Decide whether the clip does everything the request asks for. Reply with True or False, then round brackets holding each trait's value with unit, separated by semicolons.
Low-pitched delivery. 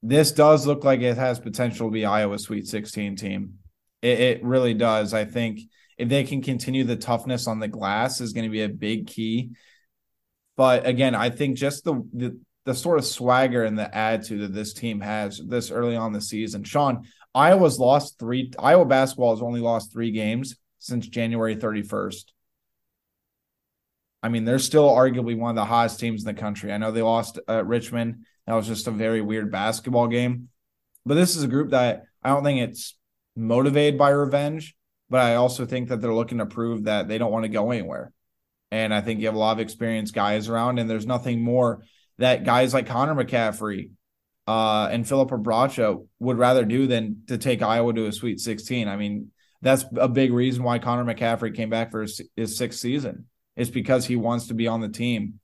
True (115 Hz)